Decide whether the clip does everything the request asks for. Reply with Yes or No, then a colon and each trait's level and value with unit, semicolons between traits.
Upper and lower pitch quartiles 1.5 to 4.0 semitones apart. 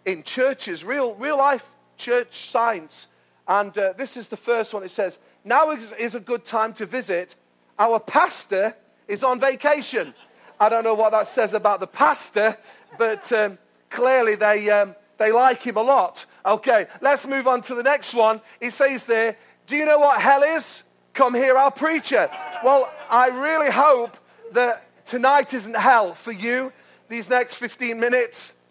Yes: average, 3.7 semitones